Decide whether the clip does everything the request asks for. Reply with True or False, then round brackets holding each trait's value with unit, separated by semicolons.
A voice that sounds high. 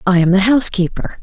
True (200 Hz)